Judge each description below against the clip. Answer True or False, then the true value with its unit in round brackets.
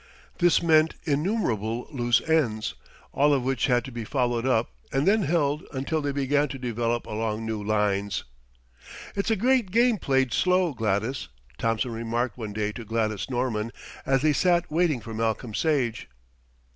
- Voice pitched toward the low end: True (125 Hz)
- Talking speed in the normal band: True (160 wpm)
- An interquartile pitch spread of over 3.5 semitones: True (5.4 semitones)